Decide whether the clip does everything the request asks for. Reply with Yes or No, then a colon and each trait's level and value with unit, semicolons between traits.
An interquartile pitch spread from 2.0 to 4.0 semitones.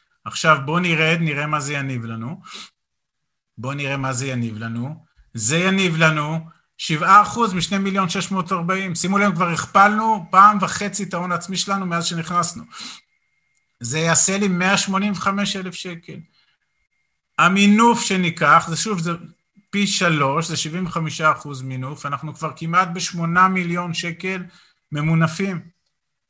Yes: average, 3.5 semitones